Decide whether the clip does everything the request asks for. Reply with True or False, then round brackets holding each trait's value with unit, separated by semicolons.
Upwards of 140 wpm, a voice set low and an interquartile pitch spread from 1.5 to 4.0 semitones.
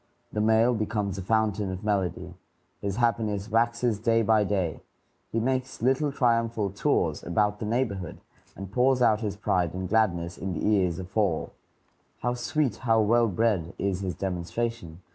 True (160 wpm; 105 Hz; 3.4 semitones)